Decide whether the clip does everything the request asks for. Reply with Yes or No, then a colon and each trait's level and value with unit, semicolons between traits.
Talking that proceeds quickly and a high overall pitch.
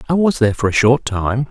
No: fast, 280 wpm; low, 125 Hz